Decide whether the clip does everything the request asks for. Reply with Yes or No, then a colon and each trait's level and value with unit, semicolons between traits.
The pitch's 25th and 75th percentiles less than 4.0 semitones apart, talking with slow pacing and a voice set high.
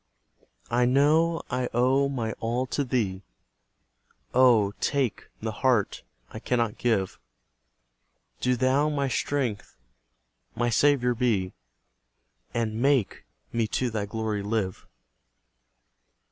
No: average, 3.1 semitones; slow, 105 wpm; low, 120 Hz